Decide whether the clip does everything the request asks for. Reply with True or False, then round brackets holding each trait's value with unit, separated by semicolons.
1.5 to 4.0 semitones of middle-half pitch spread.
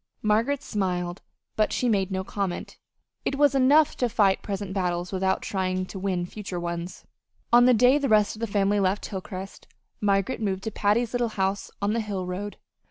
True (3.0 semitones)